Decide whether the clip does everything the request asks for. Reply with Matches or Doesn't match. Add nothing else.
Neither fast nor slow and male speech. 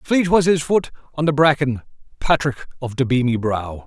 Matches